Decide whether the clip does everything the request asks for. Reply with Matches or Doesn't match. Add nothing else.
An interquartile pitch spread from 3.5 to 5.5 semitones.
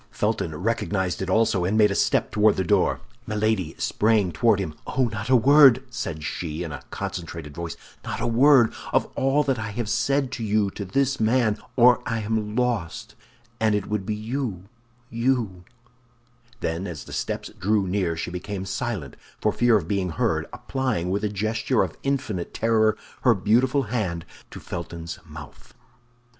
Matches